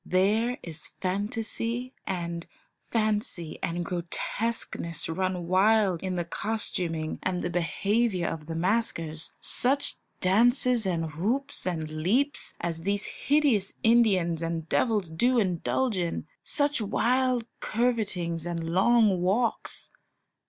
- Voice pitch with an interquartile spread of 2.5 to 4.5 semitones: No, average, 5.3 semitones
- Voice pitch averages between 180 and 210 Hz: Yes, high, 190 Hz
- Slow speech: Yes, slow, 115 wpm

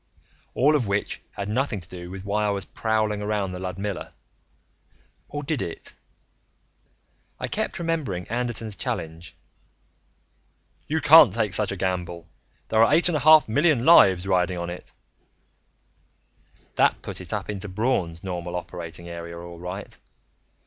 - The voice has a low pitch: Yes, low, 100 Hz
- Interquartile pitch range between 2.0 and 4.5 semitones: No, average, 4.9 semitones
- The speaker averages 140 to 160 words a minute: Yes, average, 150 wpm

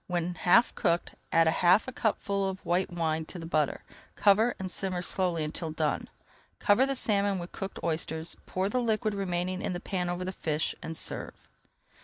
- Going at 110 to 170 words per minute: No, average, 185 wpm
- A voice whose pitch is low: No, medium, 180 Hz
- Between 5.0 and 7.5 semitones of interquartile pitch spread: No, average, 3.0 semitones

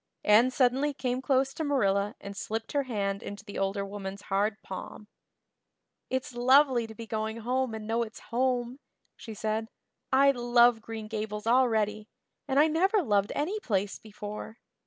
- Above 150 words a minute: Yes, average, 160 wpm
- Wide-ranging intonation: No, average, 3.6 semitones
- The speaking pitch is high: Yes, high, 225 Hz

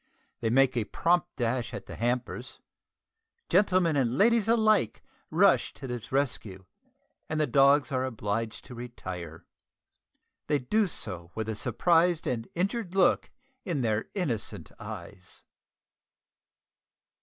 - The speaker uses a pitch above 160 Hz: No, low, 130 Hz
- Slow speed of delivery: Yes, slow, 125 wpm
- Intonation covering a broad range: Yes, wide, 7.3 semitones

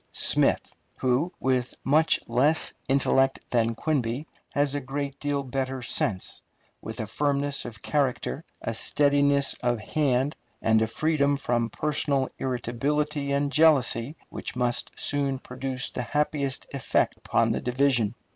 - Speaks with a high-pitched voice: No, low, 135 Hz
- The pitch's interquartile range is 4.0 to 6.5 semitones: No, average, 2.7 semitones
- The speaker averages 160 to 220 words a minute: No, slow, 135 wpm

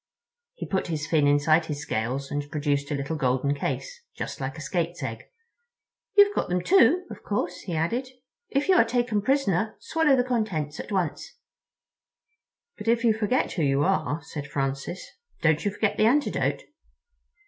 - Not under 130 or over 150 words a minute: No, average, 170 wpm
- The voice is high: No, medium, 175 Hz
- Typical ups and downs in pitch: No, wide, 8.3 semitones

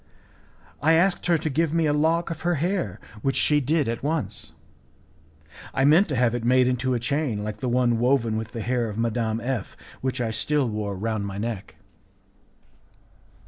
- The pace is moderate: Yes, average, 185 wpm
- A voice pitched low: Yes, low, 125 Hz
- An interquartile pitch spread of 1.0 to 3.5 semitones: No, average, 4.9 semitones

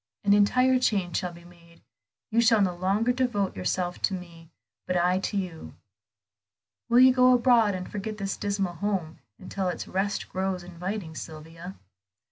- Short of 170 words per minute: Yes, average, 160 wpm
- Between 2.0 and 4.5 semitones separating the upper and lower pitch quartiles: Yes, average, 3.1 semitones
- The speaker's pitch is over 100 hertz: Yes, high, 190 Hz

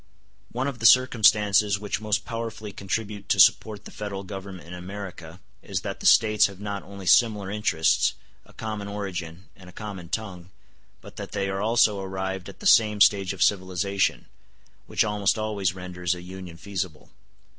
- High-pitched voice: No, low, 100 Hz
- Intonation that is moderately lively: No, narrow, 2.3 semitones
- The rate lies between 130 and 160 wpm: No, average, 170 wpm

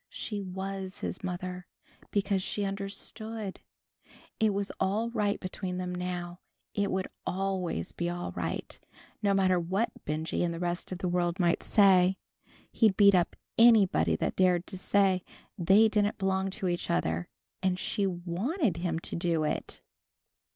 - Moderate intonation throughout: No, narrow, 2.3 semitones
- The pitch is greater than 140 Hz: Yes, medium, 185 Hz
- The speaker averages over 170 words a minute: No, average, 155 wpm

